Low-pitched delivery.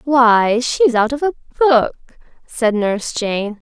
No: high, 245 Hz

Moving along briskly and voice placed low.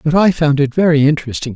No: fast, 230 wpm; medium, 150 Hz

